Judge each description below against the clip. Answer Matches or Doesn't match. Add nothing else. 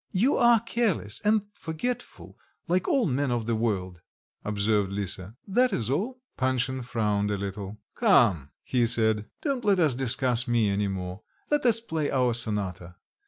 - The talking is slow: Doesn't match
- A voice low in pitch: Matches